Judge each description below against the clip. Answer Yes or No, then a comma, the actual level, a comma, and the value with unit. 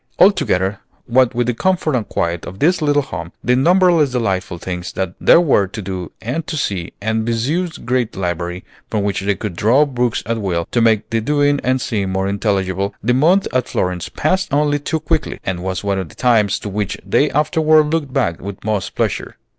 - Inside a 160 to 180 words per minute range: No, average, 200 wpm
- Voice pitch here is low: Yes, low, 115 Hz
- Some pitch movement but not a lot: No, wide, 7.1 semitones